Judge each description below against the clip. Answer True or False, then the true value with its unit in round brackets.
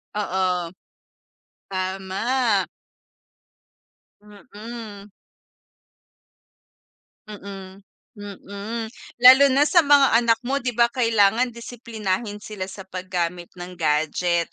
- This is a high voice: True (205 Hz)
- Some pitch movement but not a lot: True (3.9 semitones)